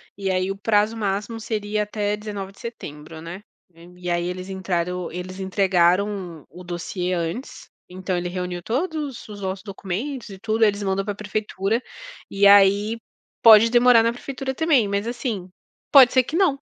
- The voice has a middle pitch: No, high, 200 Hz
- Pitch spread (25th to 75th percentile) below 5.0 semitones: Yes, average, 3.7 semitones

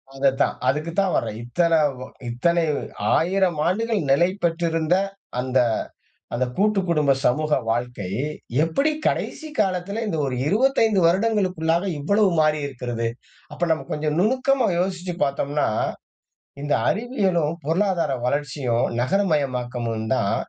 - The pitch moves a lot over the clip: Yes, wide, 5.9 semitones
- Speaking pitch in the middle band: Yes, medium, 165 Hz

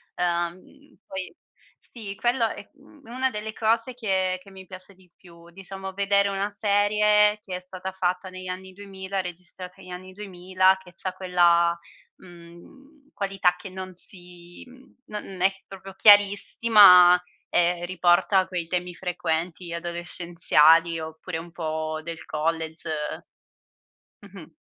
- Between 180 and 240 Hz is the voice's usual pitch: Yes, medium, 185 Hz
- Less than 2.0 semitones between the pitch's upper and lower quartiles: No, narrow, 2.3 semitones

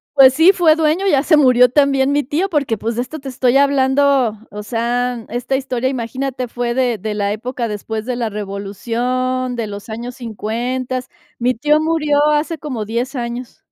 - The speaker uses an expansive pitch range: No, average, 3.2 semitones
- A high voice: Yes, very high, 255 Hz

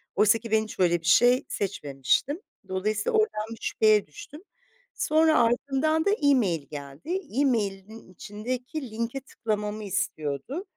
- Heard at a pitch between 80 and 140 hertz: No, high, 220 Hz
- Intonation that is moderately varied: No, wide, 5.9 semitones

